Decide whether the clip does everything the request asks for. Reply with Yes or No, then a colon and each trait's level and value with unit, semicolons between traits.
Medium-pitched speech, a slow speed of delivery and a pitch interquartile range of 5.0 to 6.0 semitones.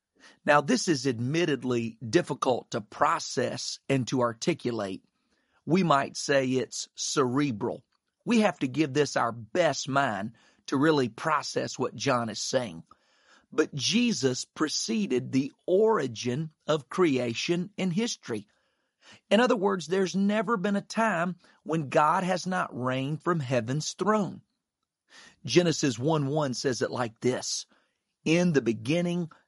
Yes: medium, 155 Hz; slow, 130 wpm; wide, 5.6 semitones